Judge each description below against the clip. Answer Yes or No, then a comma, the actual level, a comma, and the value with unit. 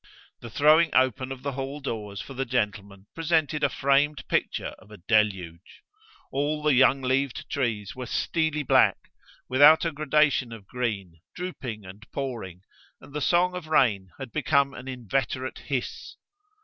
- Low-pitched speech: Yes, low, 130 Hz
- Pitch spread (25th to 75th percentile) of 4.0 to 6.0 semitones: Yes, average, 5.2 semitones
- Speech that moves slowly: No, average, 155 wpm